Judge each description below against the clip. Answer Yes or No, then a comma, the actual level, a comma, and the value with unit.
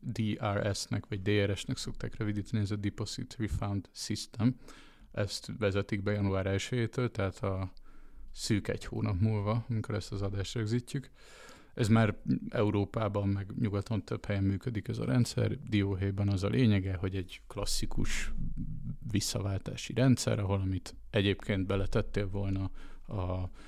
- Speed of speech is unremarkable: Yes, average, 130 wpm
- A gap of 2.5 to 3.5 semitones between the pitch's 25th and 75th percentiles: Yes, average, 2.9 semitones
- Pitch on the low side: Yes, low, 105 Hz